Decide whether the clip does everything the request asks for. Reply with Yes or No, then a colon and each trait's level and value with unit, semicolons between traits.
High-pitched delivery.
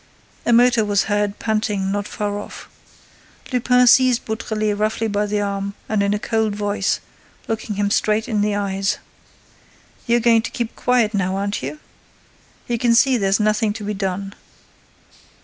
Yes: high, 210 Hz